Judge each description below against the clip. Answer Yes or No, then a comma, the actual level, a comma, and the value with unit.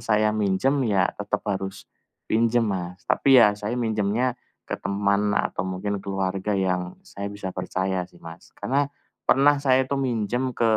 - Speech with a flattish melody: No, average, 3.8 semitones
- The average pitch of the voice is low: Yes, low, 105 Hz